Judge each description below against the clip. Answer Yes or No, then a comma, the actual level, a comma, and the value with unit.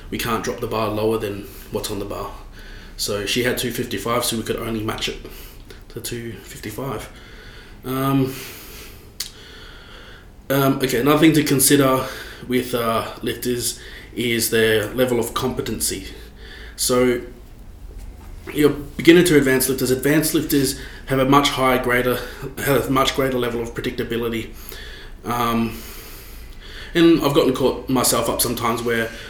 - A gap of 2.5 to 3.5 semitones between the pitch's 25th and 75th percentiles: Yes, average, 2.9 semitones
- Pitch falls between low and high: No, low, 120 Hz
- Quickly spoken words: No, slow, 135 wpm